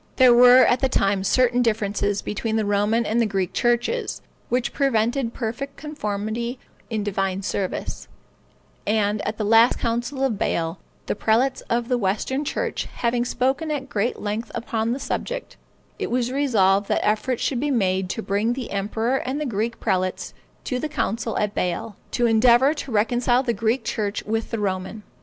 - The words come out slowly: No, average, 175 wpm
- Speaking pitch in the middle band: No, high, 230 Hz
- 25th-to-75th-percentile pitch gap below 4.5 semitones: Yes, average, 3.4 semitones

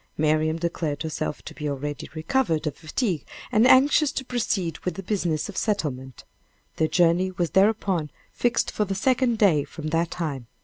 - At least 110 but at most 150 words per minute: No, average, 170 wpm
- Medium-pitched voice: Yes, medium, 170 Hz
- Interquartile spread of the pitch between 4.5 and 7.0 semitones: Yes, average, 5.2 semitones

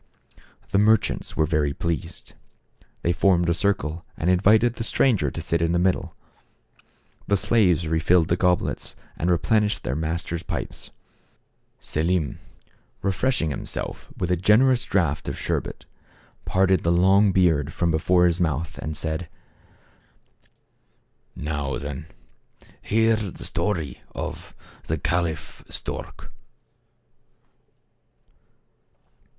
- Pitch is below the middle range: Yes, very low, 85 Hz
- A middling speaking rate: No, slow, 115 wpm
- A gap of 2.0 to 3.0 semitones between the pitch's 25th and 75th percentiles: No, average, 3.6 semitones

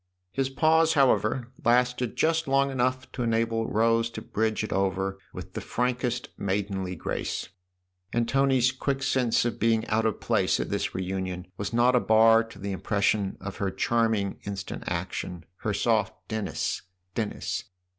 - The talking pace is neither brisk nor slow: Yes, average, 165 wpm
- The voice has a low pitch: Yes, low, 115 Hz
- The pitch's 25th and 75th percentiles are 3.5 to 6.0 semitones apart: Yes, average, 3.8 semitones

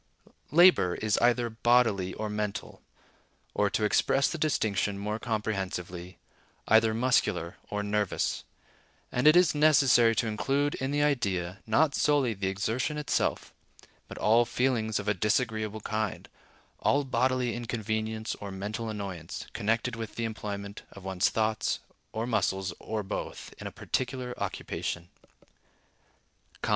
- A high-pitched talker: No, low, 110 Hz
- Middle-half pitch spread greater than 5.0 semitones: No, average, 3.5 semitones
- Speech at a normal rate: No, slow, 130 wpm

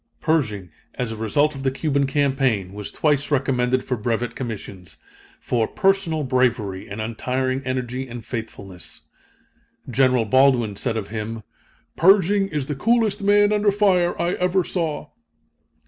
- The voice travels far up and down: Yes, wide, 6.1 semitones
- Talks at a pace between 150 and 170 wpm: No, average, 140 wpm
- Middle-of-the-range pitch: No, low, 130 Hz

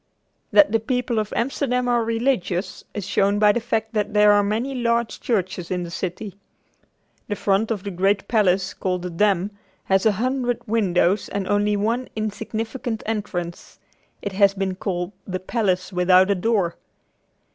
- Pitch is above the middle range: Yes, high, 205 Hz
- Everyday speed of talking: Yes, average, 170 wpm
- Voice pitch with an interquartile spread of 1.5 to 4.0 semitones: Yes, average, 3.2 semitones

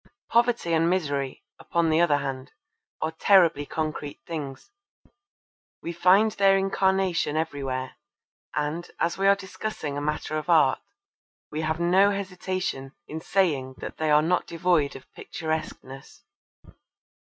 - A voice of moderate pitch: Yes, medium, 160 Hz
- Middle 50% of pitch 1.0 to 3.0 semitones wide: No, average, 4.1 semitones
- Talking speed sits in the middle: No, slow, 130 wpm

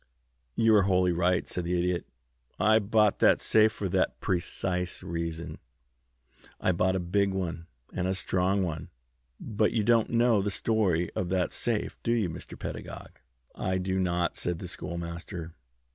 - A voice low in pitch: Yes, very low, 90 Hz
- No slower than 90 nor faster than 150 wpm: No, average, 165 wpm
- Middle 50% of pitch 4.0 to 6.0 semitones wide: No, average, 3.0 semitones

